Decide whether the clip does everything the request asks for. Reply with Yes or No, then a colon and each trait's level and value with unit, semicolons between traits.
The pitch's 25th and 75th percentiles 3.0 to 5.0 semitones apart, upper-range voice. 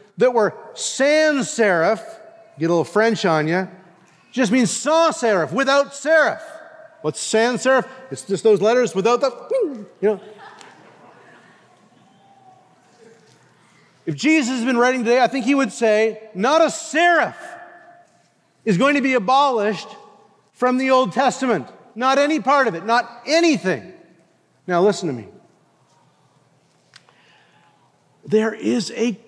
No: wide, 5.5 semitones; high, 245 Hz